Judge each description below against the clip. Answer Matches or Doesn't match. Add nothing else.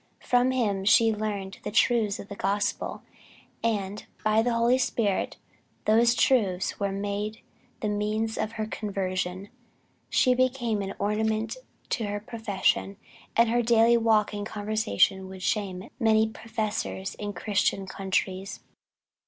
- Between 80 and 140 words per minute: Matches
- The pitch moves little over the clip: Matches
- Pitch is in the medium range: Doesn't match